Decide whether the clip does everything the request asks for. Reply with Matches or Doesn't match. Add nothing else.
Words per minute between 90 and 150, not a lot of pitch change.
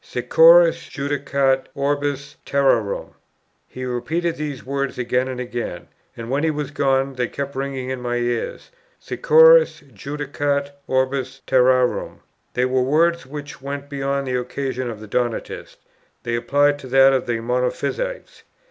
Matches